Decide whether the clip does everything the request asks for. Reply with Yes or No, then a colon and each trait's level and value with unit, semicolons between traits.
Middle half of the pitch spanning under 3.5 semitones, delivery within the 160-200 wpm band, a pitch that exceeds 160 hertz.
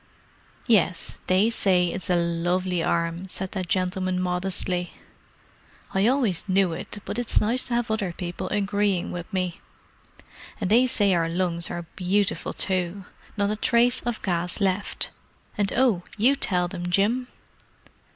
No: average, 2.9 semitones; average, 145 wpm; high, 190 Hz